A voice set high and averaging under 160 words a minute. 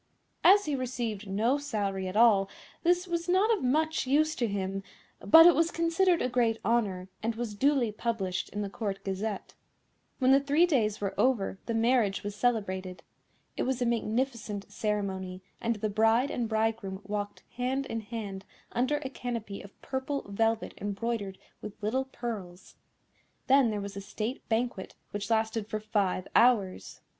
No: high, 225 Hz; average, 165 wpm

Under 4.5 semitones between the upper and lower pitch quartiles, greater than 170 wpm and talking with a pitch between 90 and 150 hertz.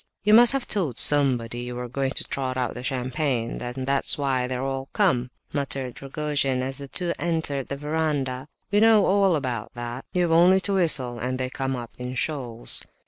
Yes: average, 4.1 semitones; average, 195 wpm; low, 135 Hz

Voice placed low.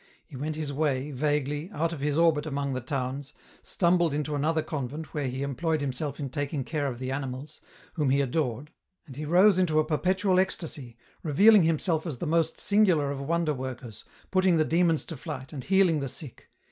No: medium, 150 Hz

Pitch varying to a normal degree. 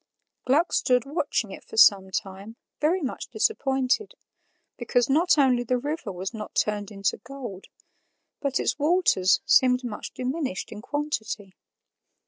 No: wide, 5.7 semitones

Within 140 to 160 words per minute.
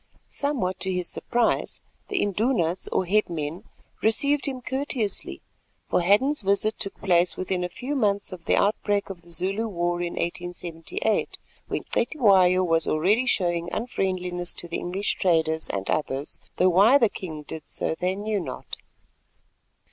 Yes: average, 150 wpm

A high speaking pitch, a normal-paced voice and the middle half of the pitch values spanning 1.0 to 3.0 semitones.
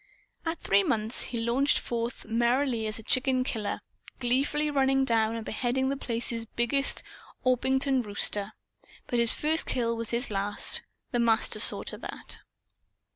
Yes: high, 240 Hz; average, 150 wpm; average, 2.7 semitones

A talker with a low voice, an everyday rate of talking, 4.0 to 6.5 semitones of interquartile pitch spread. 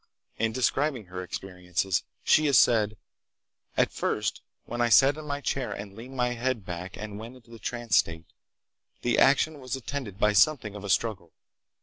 Yes: low, 115 Hz; average, 180 wpm; average, 4.7 semitones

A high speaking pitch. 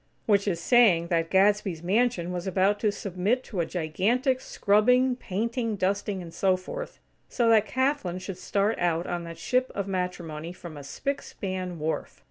Yes: high, 195 Hz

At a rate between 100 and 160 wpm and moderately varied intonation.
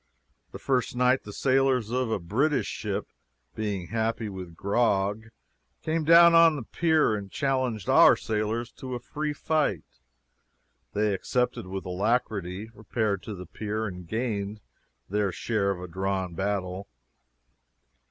Yes: average, 140 wpm; average, 4.6 semitones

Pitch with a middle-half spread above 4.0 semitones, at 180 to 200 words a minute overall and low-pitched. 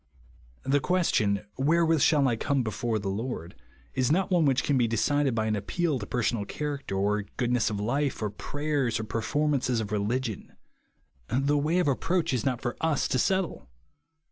Yes: average, 5.1 semitones; average, 185 wpm; low, 130 Hz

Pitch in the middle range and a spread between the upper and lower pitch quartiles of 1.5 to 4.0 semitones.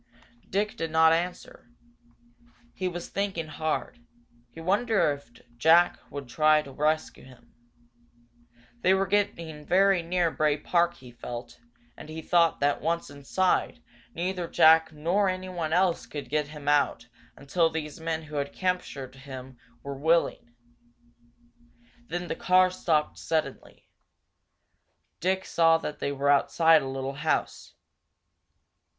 Yes: medium, 160 Hz; average, 3.7 semitones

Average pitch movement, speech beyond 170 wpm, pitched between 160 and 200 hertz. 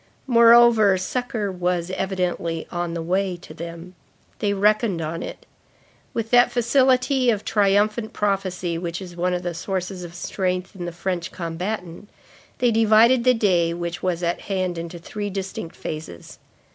No: average, 3.8 semitones; average, 155 wpm; medium, 185 Hz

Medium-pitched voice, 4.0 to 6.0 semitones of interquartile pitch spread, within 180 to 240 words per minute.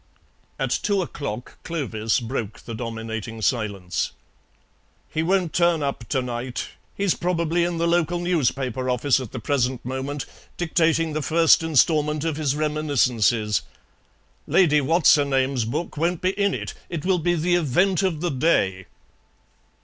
No: medium, 150 Hz; average, 5.3 semitones; average, 150 wpm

